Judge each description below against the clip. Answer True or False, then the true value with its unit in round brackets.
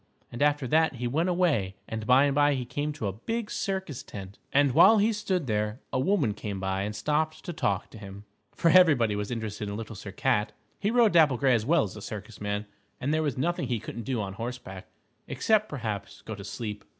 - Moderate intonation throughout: False (6.9 semitones)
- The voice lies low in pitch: True (125 Hz)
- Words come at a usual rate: False (225 wpm)